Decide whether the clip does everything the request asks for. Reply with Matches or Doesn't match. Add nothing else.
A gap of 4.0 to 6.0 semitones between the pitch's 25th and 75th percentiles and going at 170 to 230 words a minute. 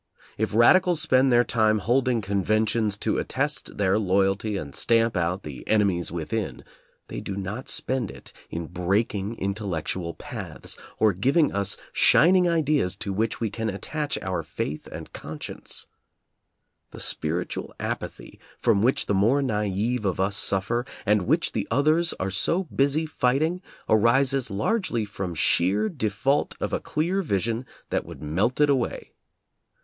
Doesn't match